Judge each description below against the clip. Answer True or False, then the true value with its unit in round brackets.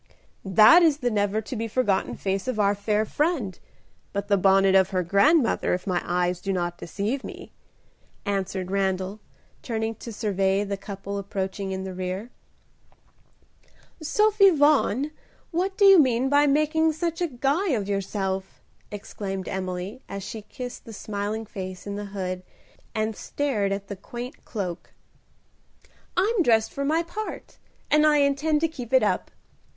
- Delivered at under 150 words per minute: False (155 wpm)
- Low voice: False (210 Hz)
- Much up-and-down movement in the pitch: True (6.4 semitones)